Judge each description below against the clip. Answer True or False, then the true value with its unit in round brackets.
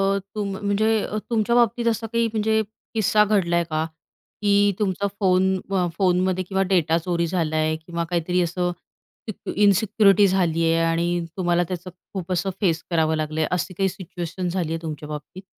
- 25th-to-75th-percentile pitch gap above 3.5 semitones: False (3.2 semitones)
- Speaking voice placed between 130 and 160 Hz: False (185 Hz)